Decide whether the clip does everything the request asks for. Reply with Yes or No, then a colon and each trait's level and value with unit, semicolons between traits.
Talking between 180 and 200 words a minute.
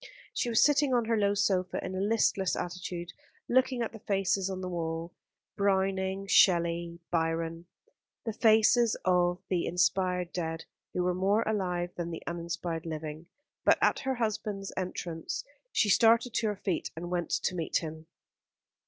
No: average, 160 wpm